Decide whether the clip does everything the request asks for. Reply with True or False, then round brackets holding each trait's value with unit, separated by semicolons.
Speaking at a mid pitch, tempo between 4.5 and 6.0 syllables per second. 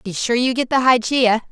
False (240 Hz; 5.0 syllables/s)